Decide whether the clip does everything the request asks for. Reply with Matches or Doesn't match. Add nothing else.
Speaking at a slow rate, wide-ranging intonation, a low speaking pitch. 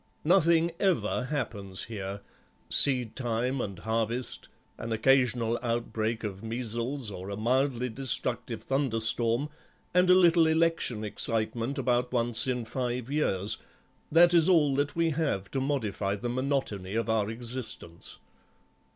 Doesn't match